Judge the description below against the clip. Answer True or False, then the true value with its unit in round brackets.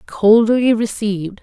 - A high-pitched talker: True (215 Hz)